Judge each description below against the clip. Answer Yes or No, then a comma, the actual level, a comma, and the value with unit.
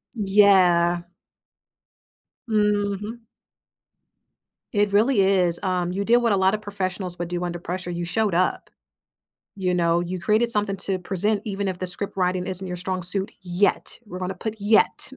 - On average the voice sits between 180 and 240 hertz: Yes, high, 190 Hz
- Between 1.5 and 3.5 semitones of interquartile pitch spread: Yes, narrow, 2.5 semitones